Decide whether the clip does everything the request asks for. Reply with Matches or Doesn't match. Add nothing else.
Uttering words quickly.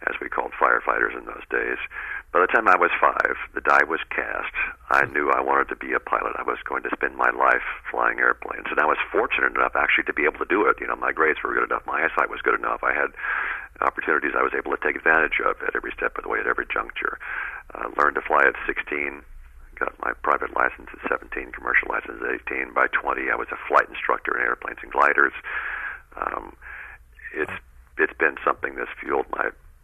Matches